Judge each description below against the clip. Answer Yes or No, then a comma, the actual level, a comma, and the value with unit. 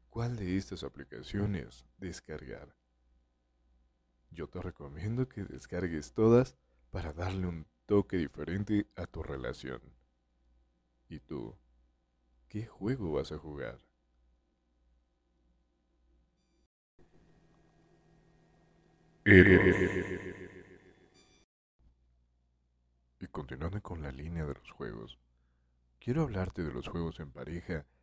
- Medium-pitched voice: No, very low, 70 Hz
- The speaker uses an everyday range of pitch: No, wide, 7.4 semitones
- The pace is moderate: No, slow, 90 wpm